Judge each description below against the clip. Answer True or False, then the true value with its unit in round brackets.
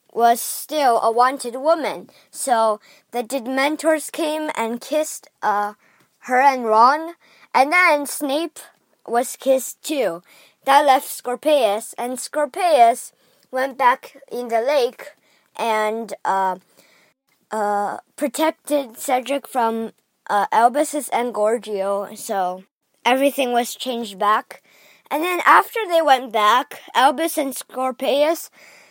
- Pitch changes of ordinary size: True (4.6 semitones)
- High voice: True (260 Hz)